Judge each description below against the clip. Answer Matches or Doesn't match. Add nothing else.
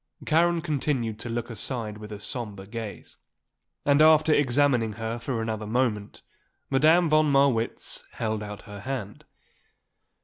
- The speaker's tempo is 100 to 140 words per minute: Matches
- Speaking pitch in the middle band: Doesn't match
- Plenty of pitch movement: Doesn't match